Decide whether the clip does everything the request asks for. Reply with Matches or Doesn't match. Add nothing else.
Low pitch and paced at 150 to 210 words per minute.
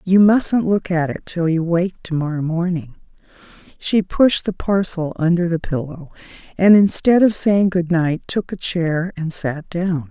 Doesn't match